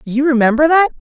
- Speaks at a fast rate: No, average, 165 wpm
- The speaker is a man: No, female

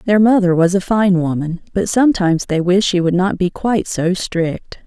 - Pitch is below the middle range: No, medium, 185 Hz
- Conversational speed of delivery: No, fast, 210 wpm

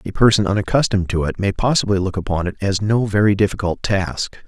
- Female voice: No, male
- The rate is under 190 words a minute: No, average, 200 wpm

